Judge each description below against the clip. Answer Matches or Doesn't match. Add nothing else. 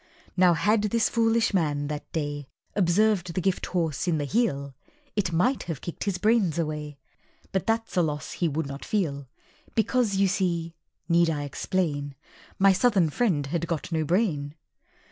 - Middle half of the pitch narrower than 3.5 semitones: Doesn't match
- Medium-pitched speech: Matches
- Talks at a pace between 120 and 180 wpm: Matches